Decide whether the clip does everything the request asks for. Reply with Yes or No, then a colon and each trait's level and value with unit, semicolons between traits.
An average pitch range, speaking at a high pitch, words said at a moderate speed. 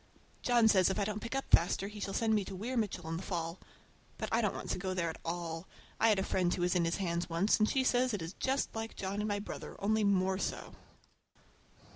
No: average, 3.6 semitones; high, 195 Hz; fast, 255 wpm